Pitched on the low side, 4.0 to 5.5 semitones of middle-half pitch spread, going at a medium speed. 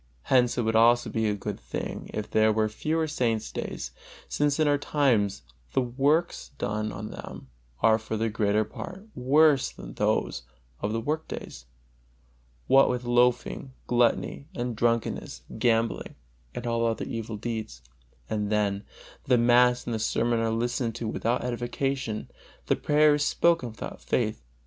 No: low, 120 Hz; average, 2.8 semitones; average, 155 wpm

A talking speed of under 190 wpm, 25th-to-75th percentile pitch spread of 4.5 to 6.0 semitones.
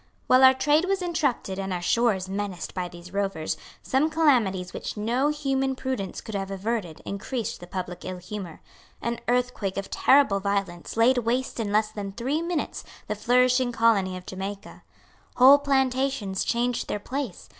Yes: average, 165 wpm; average, 5.2 semitones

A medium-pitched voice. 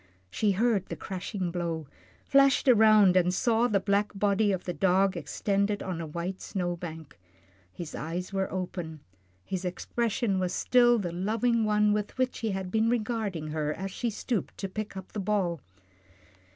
No: high, 195 Hz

